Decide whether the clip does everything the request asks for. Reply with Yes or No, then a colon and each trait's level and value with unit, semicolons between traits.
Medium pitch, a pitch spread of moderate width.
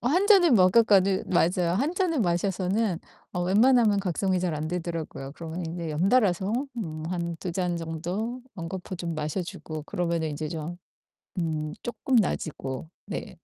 Yes: medium, 180 Hz; average, 3.7 semitones